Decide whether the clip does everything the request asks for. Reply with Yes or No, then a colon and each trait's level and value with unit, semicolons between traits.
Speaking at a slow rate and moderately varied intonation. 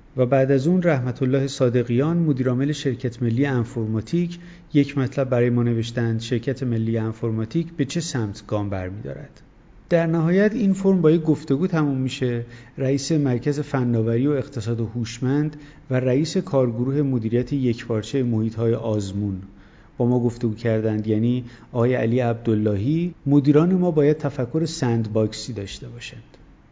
No: average, 140 wpm; average, 4.2 semitones